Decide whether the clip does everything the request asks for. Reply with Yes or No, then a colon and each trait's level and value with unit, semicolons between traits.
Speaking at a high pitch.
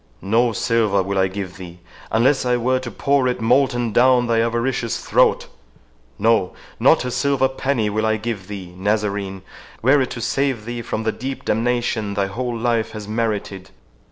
No: low, 115 Hz